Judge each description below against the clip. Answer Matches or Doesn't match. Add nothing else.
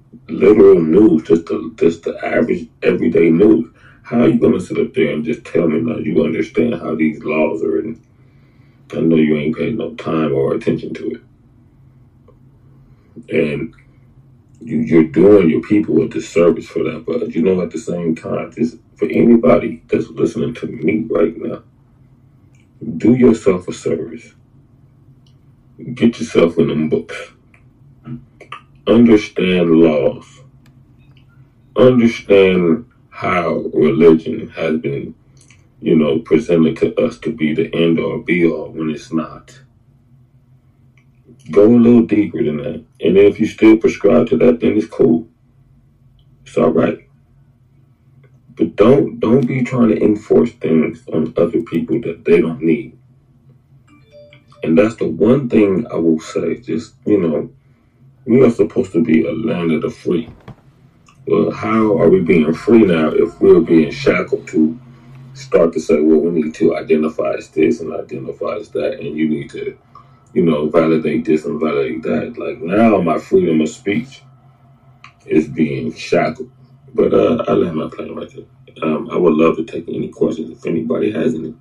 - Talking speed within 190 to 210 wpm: Doesn't match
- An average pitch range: Doesn't match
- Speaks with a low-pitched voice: Matches